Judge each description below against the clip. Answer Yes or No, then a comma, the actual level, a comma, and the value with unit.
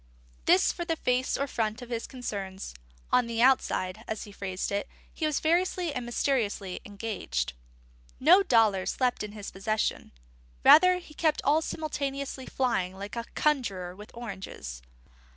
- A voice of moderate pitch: No, high, 235 Hz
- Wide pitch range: Yes, wide, 5.8 semitones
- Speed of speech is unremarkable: Yes, average, 150 wpm